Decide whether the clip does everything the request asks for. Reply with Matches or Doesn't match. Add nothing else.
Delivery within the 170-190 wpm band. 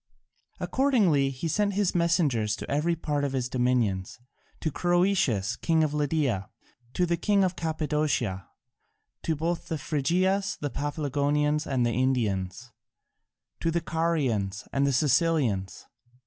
Doesn't match